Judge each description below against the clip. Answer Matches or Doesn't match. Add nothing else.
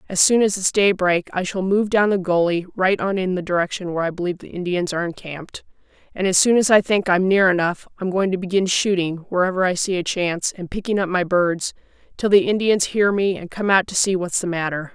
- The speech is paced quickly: Matches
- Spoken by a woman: Matches